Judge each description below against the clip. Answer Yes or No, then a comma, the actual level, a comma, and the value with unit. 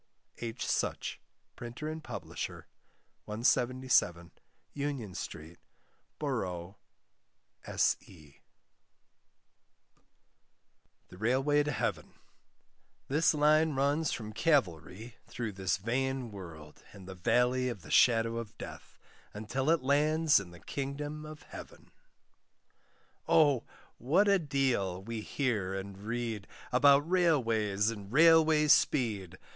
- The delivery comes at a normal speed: No, slow, 105 wpm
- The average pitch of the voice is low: Yes, low, 120 Hz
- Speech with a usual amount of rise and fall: No, wide, 6.6 semitones